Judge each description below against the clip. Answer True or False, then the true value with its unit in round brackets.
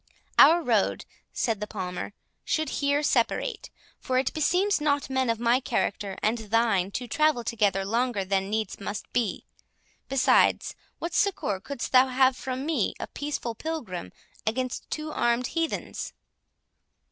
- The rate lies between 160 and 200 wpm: False (145 wpm)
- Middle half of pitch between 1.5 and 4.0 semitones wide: False (5.2 semitones)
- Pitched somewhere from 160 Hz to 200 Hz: False (245 Hz)